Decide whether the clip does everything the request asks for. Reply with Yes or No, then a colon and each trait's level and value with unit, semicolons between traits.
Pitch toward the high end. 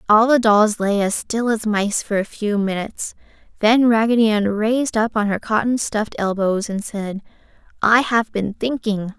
Yes: high, 215 Hz